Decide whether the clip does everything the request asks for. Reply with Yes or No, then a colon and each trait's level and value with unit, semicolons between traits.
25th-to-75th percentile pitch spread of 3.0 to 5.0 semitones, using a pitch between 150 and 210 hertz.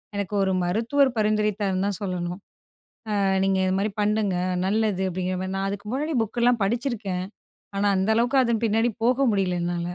Yes: average, 3.3 semitones; high, 205 Hz